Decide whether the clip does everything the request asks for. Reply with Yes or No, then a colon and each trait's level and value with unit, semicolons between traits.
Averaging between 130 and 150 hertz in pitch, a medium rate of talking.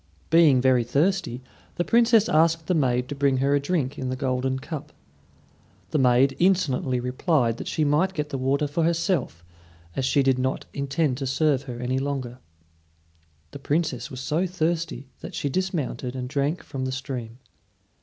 Yes: medium, 140 Hz; average, 175 wpm